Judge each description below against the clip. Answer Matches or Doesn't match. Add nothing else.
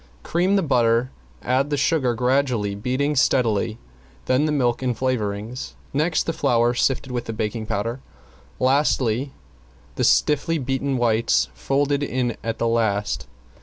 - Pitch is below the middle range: Matches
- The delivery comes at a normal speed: Matches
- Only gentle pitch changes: Doesn't match